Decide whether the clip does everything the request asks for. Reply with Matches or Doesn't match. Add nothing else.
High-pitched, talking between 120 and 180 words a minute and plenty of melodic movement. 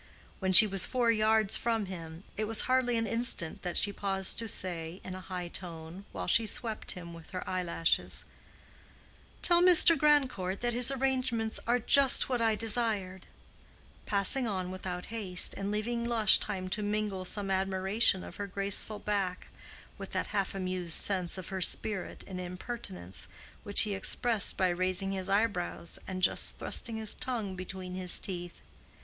Doesn't match